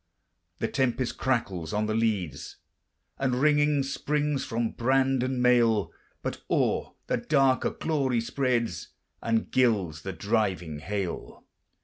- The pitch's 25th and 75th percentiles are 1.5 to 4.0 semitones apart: No, average, 4.5 semitones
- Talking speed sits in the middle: No, slow, 125 wpm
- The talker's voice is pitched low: Yes, low, 120 Hz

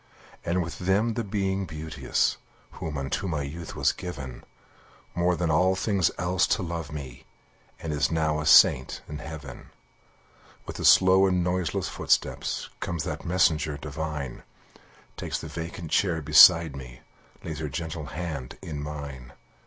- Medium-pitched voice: No, very low, 80 Hz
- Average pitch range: Yes, average, 3.3 semitones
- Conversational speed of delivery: Yes, average, 150 wpm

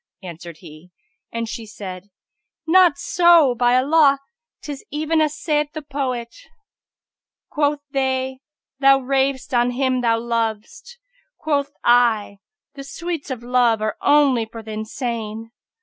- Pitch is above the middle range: Yes, very high, 255 Hz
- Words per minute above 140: No, slow, 135 wpm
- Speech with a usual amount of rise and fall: Yes, average, 4.2 semitones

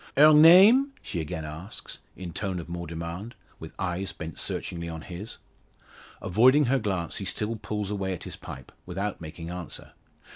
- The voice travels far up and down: No, average, 4.5 semitones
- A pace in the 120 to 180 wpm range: Yes, average, 170 wpm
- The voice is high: No, very low, 95 Hz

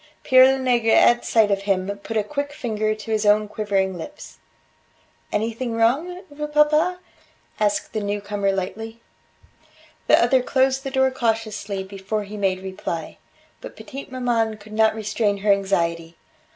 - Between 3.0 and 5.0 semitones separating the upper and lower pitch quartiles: Yes, average, 4.3 semitones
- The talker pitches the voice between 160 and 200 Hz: No, high, 215 Hz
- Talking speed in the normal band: Yes, average, 150 wpm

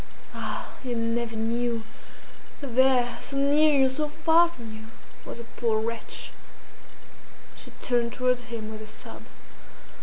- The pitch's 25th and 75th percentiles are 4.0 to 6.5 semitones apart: No, average, 2.7 semitones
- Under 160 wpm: Yes, average, 145 wpm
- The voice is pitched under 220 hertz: No, high, 240 Hz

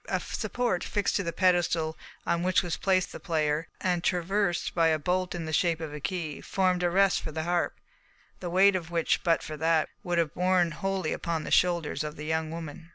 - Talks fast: Yes, fast, 220 wpm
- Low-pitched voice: No, medium, 170 Hz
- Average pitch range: No, narrow, 2.3 semitones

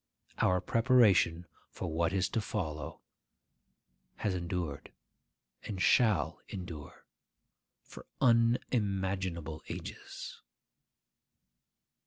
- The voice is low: Yes, very low, 95 Hz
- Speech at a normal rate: No, slow, 75 wpm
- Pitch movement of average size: Yes, average, 4.2 semitones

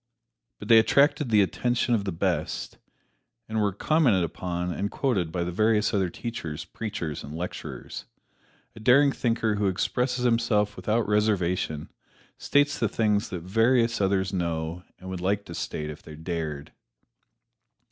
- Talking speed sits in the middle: Yes, average, 150 wpm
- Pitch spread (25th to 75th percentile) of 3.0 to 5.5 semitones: Yes, average, 4.7 semitones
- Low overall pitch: Yes, low, 100 Hz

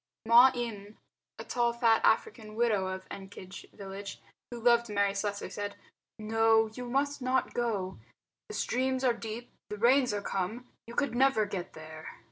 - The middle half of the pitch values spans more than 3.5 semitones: No, average, 3.2 semitones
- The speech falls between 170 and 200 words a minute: No, average, 160 wpm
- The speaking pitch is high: Yes, high, 225 Hz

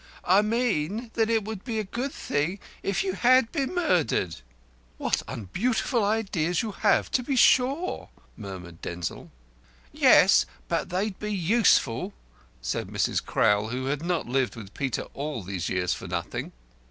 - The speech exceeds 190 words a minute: No, average, 155 wpm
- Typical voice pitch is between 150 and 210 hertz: Yes, high, 190 Hz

